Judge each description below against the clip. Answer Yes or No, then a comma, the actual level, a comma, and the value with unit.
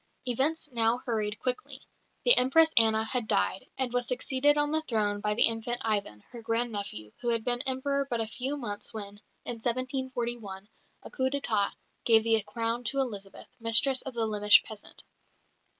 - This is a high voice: Yes, high, 235 Hz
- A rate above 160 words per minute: Yes, average, 170 wpm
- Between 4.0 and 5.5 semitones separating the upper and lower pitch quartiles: No, average, 3.3 semitones